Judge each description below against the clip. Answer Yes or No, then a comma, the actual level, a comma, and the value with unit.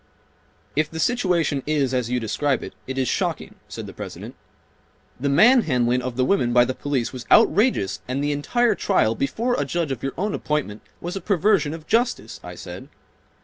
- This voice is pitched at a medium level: Yes, medium, 145 Hz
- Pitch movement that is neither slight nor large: No, wide, 6.6 semitones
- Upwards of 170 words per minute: Yes, average, 190 wpm